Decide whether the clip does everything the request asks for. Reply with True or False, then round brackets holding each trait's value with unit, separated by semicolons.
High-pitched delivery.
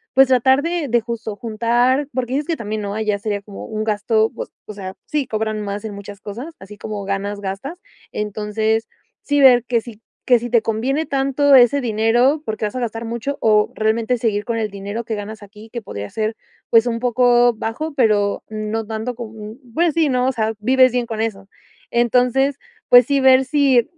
True (225 Hz)